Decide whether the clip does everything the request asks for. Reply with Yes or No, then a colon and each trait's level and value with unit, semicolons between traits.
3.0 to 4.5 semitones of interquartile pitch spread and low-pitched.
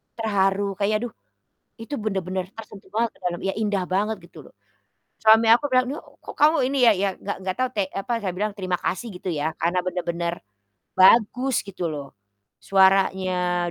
No: average, 3.3 semitones; high, 195 Hz